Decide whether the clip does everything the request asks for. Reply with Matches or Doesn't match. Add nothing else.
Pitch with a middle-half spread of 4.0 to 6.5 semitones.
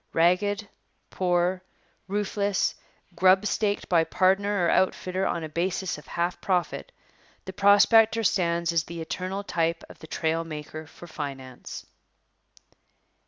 Doesn't match